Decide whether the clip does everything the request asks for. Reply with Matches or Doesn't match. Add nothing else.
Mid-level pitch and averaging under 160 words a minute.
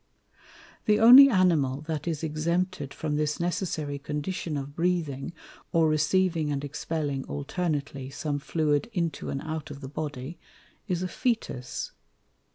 Matches